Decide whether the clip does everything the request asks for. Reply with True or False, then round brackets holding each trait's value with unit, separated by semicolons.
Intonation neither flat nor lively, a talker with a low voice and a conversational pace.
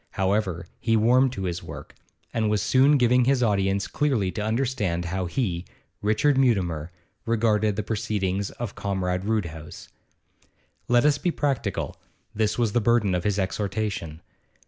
True (4.1 semitones; 105 Hz; 145 wpm)